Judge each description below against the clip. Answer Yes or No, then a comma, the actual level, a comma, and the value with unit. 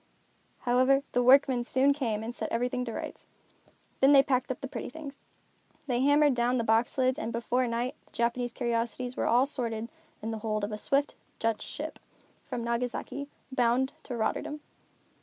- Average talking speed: Yes, average, 175 wpm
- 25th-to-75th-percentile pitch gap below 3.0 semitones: Yes, narrow, 2.4 semitones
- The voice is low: No, high, 245 Hz